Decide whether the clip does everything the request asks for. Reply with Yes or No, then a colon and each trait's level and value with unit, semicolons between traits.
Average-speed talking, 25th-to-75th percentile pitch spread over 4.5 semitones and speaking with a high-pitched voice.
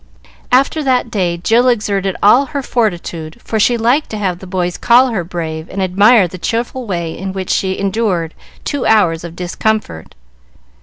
Yes: average, 170 wpm; average, 5.0 semitones; high, 195 Hz